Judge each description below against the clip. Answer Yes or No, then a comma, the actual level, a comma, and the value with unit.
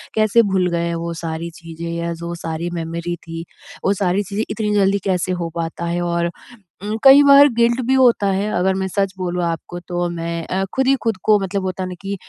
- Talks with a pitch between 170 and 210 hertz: Yes, medium, 185 Hz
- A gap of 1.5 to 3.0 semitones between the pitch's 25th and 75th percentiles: No, average, 3.4 semitones